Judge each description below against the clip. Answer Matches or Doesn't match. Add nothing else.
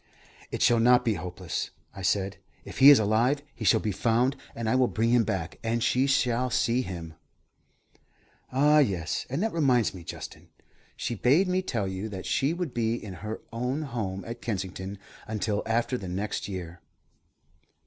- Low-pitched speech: Matches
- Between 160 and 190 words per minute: Matches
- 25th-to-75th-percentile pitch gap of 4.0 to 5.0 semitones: Matches